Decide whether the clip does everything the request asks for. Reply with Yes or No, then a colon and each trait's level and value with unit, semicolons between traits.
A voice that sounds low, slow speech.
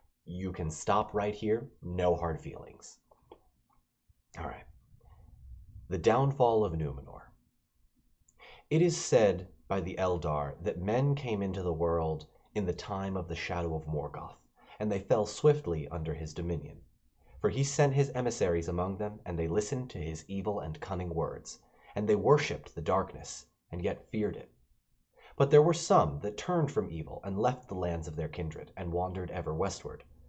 No: very low, 95 Hz; average, 170 wpm